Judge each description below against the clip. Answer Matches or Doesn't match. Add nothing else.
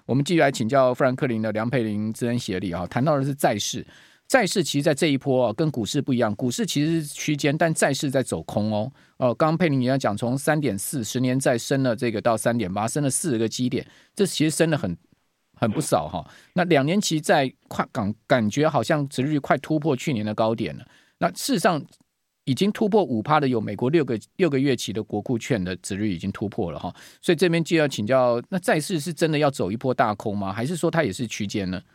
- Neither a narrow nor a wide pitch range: Doesn't match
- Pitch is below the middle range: Matches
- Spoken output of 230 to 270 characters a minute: Doesn't match